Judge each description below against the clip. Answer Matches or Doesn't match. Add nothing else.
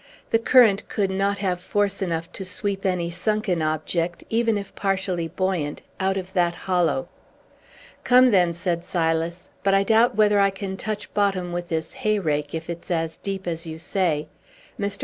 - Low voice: Doesn't match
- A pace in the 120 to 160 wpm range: Doesn't match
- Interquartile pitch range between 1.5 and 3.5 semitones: Matches